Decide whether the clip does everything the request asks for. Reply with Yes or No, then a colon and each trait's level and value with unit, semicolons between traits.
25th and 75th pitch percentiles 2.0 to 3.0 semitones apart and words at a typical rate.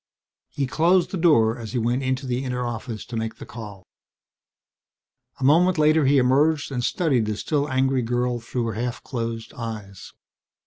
No: average, 3.7 semitones; average, 170 wpm